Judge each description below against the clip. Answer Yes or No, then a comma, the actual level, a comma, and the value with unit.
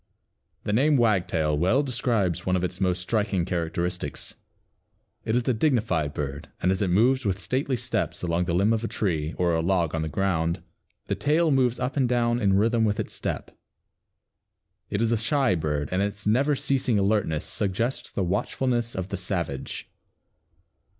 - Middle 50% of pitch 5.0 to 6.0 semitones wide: Yes, average, 5.3 semitones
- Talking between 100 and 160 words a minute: No, average, 175 wpm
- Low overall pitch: Yes, low, 100 Hz